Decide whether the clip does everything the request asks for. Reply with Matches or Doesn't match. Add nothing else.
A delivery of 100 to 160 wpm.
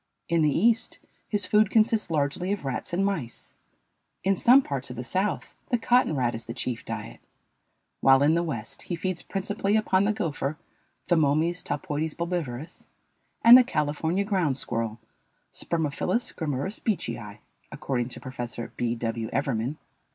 Matches